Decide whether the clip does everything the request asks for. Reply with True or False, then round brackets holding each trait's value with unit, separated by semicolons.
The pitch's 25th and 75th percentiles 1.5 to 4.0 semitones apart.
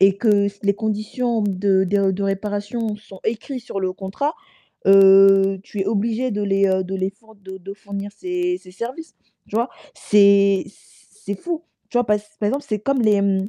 True (2.4 semitones)